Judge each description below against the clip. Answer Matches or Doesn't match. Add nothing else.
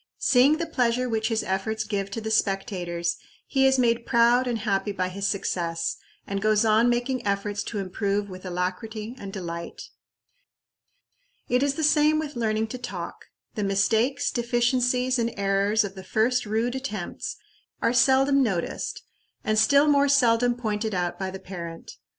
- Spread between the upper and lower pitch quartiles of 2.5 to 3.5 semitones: Doesn't match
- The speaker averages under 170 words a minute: Matches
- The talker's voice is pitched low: Doesn't match